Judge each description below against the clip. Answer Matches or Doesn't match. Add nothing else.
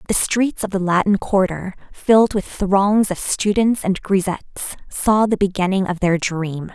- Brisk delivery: Doesn't match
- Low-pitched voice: Doesn't match